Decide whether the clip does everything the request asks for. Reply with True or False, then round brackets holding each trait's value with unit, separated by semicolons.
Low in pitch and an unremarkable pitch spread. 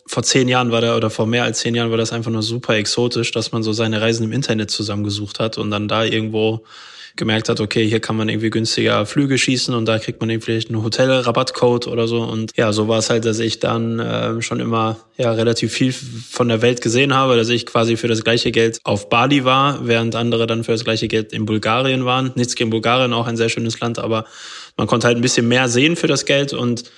False (115 Hz; 1.4 semitones)